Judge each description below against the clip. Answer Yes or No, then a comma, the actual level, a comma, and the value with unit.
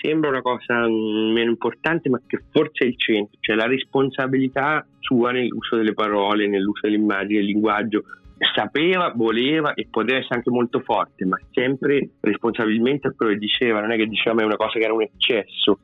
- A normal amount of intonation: Yes, average, 3.4 semitones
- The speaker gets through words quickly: Yes, fast, 180 wpm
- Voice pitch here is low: Yes, low, 115 Hz